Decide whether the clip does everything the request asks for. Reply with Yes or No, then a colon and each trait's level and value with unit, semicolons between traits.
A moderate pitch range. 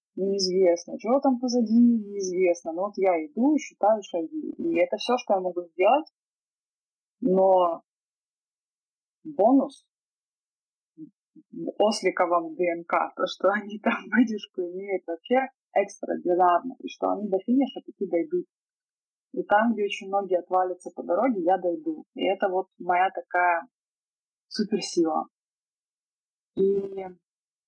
No: wide, 6.2 semitones